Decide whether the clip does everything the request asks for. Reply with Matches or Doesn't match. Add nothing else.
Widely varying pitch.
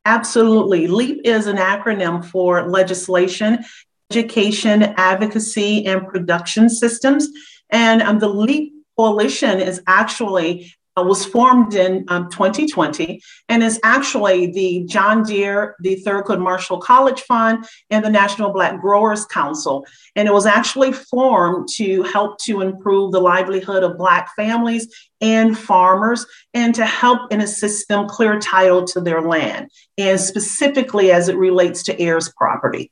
Doesn't match